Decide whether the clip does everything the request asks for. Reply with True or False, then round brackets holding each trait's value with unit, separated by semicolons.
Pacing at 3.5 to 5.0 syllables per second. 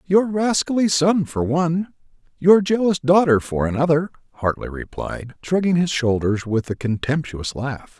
True (4.5 syllables/s)